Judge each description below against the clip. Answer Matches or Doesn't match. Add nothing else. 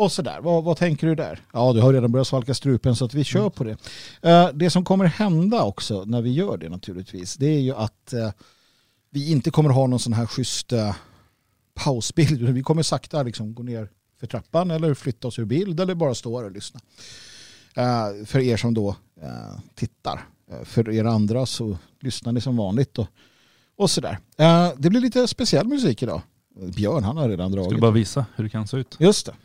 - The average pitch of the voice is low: Matches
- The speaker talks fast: Matches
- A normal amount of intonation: Doesn't match